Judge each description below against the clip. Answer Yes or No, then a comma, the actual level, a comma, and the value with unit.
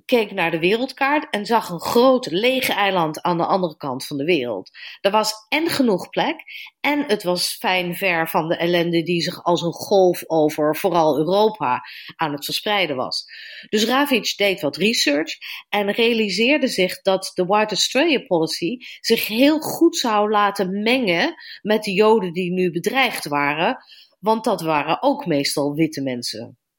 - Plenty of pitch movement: Yes, wide, 6.2 semitones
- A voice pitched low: No, high, 200 Hz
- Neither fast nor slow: Yes, average, 170 wpm